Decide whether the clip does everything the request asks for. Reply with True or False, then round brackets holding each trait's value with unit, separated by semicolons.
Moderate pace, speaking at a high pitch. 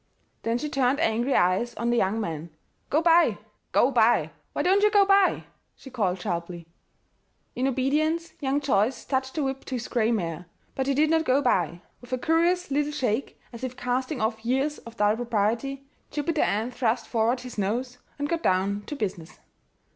True (185 wpm; 250 Hz)